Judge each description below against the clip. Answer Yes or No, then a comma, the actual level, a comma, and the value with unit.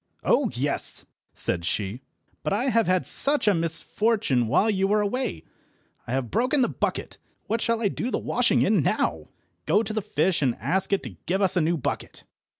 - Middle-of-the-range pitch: No, high, 195 Hz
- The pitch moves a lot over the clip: Yes, wide, 7.1 semitones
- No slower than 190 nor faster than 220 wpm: Yes, average, 195 wpm